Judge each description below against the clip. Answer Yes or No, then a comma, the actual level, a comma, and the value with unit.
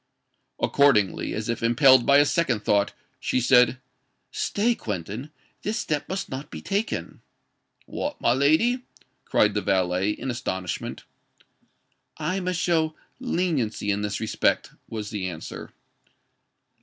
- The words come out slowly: Yes, slow, 130 wpm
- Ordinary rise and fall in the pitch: No, wide, 7.8 semitones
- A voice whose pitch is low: Yes, low, 125 Hz